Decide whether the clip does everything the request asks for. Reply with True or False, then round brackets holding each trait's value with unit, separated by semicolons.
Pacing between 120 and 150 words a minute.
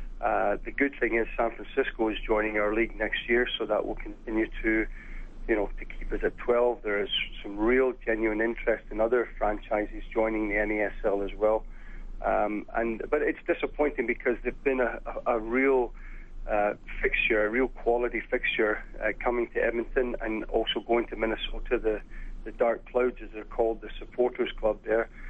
False (185 wpm)